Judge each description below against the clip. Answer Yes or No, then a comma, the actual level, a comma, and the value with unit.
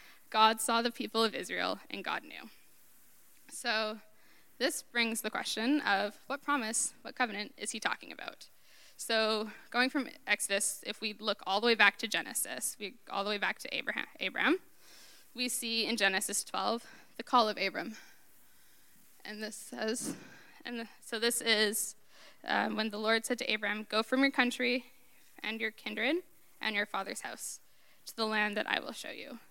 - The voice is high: Yes, high, 225 Hz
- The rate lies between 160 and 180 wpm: Yes, average, 175 wpm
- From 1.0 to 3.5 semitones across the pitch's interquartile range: Yes, average, 2.7 semitones